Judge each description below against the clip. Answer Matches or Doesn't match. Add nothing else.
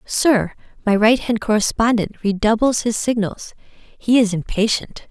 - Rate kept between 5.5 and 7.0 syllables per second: Doesn't match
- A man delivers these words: Doesn't match